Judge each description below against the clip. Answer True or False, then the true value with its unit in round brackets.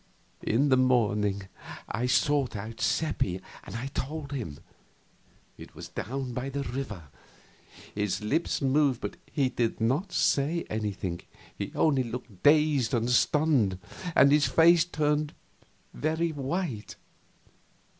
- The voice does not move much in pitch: False (4.9 semitones)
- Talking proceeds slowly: True (125 wpm)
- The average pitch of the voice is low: True (130 Hz)